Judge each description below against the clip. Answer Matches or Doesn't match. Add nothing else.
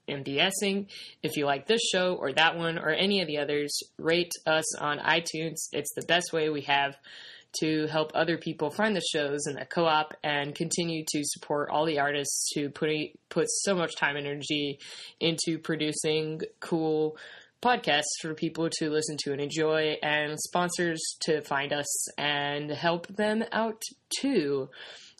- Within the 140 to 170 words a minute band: Matches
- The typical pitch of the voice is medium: Matches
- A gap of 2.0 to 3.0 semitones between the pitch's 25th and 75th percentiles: Matches